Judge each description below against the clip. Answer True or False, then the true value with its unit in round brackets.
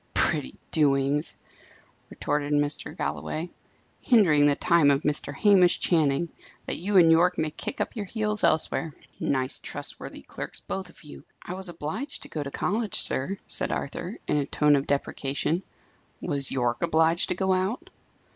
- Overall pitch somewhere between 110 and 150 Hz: False (160 Hz)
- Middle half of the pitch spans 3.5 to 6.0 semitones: True (4.4 semitones)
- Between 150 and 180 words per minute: True (160 wpm)